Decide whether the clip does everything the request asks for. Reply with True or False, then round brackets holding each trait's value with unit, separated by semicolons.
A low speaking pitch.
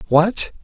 False (185 Hz)